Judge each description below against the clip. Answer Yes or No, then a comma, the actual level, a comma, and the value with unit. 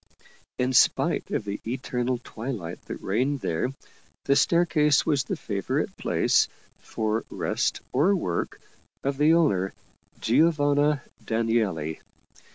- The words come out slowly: Yes, slow, 115 wpm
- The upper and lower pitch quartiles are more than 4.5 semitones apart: Yes, average, 5.2 semitones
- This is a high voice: No, low, 130 Hz